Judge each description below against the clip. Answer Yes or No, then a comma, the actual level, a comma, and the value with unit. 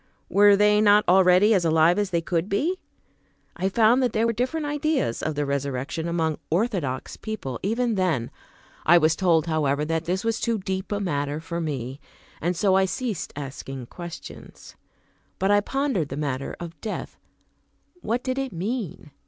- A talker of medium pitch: Yes, medium, 180 Hz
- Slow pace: No, average, 170 wpm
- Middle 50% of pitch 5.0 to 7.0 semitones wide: Yes, wide, 5.5 semitones